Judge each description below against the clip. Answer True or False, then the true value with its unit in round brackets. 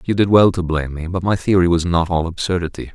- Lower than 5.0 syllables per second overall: False (6.3 syllables/s)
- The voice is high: False (90 Hz)